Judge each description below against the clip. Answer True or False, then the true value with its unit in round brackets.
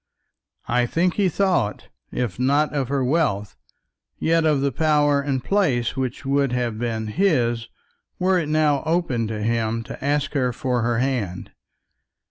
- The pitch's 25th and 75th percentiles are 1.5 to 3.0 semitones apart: False (4.5 semitones)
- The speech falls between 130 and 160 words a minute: True (155 wpm)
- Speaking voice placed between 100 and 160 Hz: True (135 Hz)